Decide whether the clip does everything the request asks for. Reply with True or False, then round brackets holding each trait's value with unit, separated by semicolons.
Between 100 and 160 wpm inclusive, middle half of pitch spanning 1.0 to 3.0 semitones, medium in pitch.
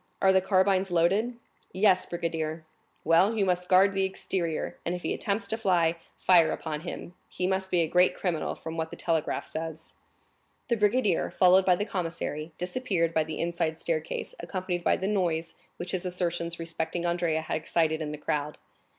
False (175 wpm; 2.6 semitones; 175 Hz)